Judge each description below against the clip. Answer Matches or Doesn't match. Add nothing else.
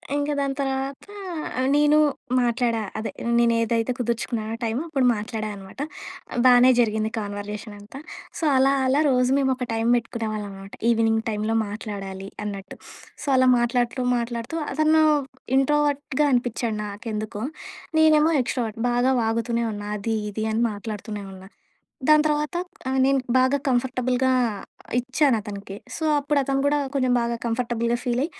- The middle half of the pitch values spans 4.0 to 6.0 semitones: Doesn't match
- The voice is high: Matches